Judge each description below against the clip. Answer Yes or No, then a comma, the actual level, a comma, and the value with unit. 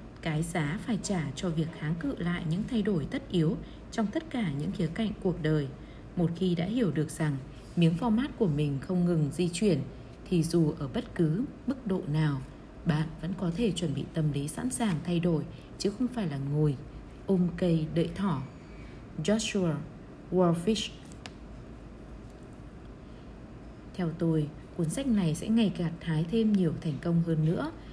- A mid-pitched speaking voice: Yes, medium, 170 Hz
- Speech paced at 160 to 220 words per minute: Yes, average, 175 wpm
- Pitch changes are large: No, average, 3.9 semitones